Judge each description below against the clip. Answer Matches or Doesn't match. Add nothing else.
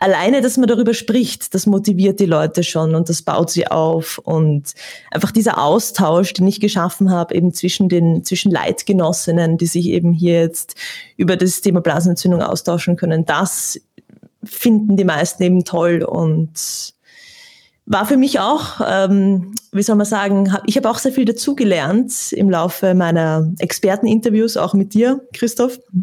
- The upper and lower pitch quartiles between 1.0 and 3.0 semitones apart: Doesn't match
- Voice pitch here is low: Doesn't match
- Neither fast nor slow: Matches